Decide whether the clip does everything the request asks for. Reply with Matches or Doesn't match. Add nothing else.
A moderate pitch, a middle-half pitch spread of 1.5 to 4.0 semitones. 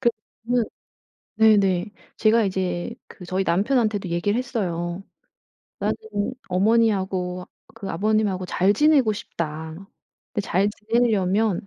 Doesn't match